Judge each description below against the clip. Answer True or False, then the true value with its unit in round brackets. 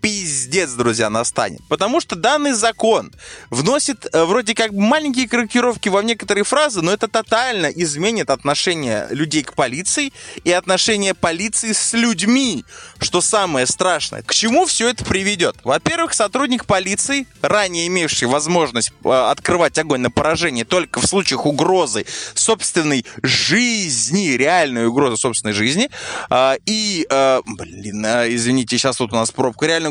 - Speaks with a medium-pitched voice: True (180 Hz)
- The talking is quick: False (140 wpm)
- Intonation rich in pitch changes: True (9.0 semitones)